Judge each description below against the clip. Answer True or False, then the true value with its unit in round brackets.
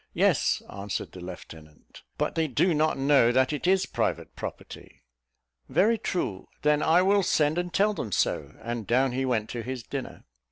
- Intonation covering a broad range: True (6.4 semitones)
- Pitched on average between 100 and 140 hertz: True (135 Hz)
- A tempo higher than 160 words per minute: True (175 wpm)